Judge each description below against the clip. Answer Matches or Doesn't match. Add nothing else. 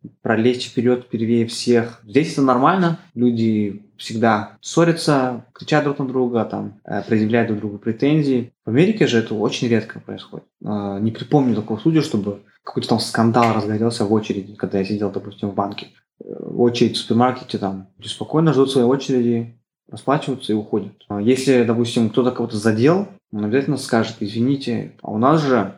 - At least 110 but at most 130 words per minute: Doesn't match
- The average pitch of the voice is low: Matches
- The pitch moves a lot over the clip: Doesn't match